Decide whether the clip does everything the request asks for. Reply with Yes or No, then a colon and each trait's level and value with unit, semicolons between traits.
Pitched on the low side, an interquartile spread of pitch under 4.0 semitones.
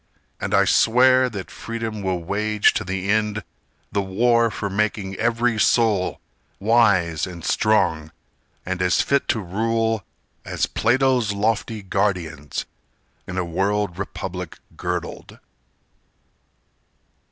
Yes: low, 105 Hz; average, 3.5 semitones